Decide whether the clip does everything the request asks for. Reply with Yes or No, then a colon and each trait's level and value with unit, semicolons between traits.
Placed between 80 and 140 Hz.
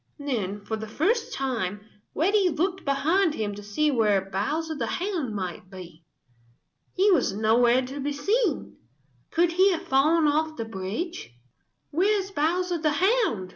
No: very high, 290 Hz